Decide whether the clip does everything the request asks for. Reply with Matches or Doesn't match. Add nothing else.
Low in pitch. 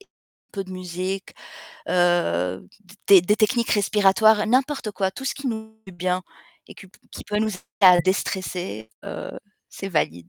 Doesn't match